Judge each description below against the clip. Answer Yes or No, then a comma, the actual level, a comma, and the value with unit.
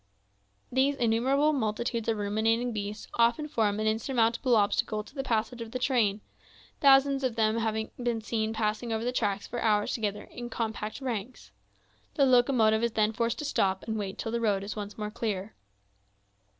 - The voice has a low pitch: No, high, 225 Hz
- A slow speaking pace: No, average, 175 wpm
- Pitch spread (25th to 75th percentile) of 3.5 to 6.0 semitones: No, narrow, 2.4 semitones